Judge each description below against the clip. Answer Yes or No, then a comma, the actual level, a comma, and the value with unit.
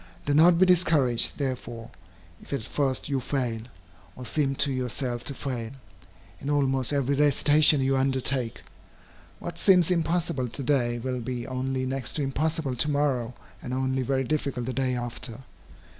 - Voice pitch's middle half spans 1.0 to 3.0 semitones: Yes, narrow, 2.6 semitones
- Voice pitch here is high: No, low, 135 Hz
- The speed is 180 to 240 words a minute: No, average, 160 wpm